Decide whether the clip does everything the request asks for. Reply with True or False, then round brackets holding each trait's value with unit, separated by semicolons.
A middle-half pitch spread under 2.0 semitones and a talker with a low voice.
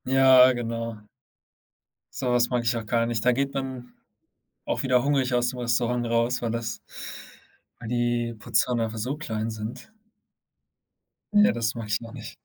True (1.5 semitones; 120 Hz)